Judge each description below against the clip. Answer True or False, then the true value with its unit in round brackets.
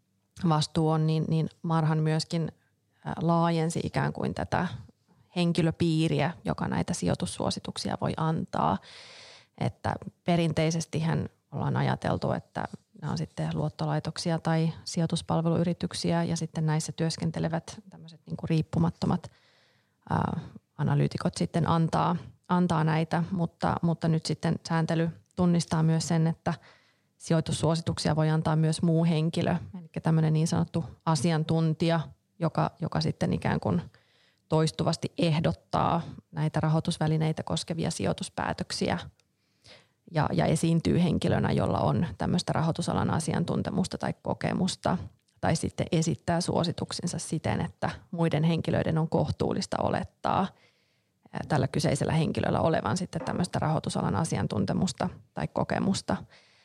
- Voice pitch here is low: False (165 Hz)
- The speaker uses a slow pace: False (110 wpm)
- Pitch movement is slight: True (1.1 semitones)